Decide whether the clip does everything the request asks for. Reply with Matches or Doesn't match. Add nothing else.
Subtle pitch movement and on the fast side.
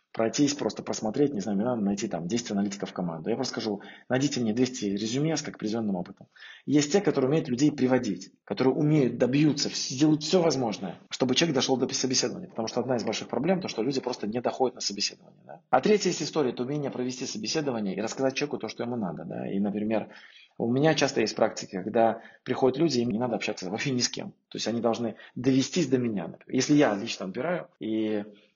Doesn't match